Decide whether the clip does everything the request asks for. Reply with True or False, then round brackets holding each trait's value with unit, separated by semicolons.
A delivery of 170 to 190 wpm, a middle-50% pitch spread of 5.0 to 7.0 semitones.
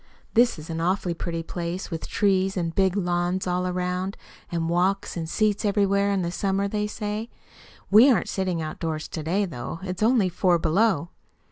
False (180 wpm; 2.7 semitones)